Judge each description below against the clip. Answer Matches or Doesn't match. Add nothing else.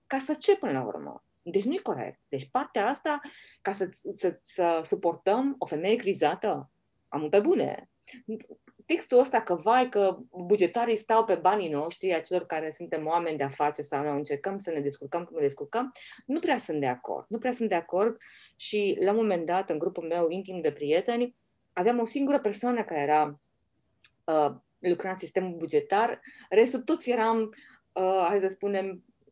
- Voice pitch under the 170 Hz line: Doesn't match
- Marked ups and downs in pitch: Matches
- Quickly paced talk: Matches